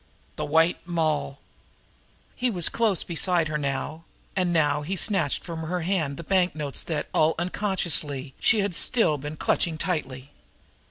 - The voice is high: No, medium, 165 Hz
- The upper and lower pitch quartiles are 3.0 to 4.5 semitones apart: Yes, average, 3.5 semitones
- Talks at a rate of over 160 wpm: No, average, 150 wpm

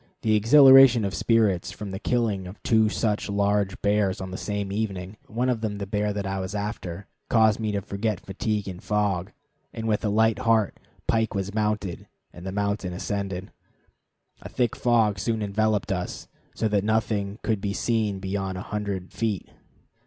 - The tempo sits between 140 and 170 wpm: No, average, 180 wpm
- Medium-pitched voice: No, low, 105 Hz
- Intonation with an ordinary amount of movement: No, narrow, 2.1 semitones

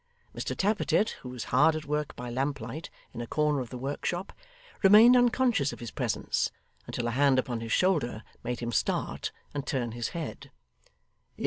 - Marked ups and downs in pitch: Yes, wide, 5.8 semitones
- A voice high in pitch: No, medium, 140 Hz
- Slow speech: No, average, 175 wpm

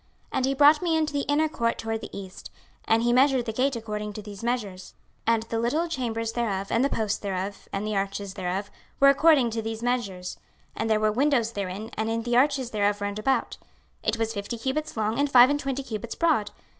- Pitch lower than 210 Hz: No, high, 230 Hz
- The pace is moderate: No, fast, 225 wpm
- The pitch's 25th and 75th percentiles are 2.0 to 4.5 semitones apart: Yes, average, 4.1 semitones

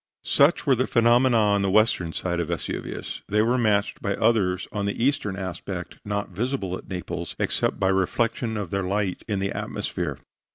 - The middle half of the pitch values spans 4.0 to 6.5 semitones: No, average, 3.5 semitones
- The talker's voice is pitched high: No, low, 100 Hz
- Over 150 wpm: Yes, average, 180 wpm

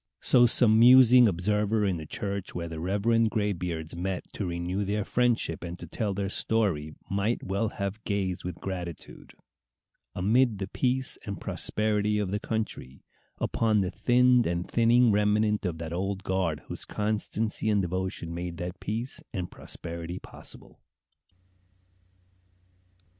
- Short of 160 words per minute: Yes, average, 140 wpm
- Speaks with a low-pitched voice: Yes, low, 100 Hz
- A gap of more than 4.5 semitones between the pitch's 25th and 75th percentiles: No, average, 3.7 semitones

